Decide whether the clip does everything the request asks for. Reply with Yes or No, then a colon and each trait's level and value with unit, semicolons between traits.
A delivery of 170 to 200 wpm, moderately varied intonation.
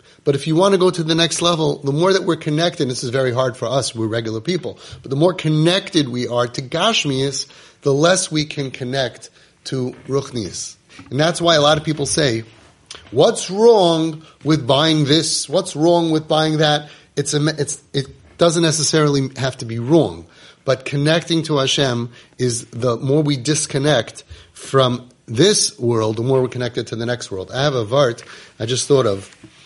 Yes: average, 195 wpm; average, 4.0 semitones